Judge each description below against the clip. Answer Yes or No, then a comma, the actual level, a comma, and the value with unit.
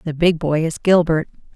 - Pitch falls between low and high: Yes, medium, 165 Hz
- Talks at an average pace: Yes, average, 195 wpm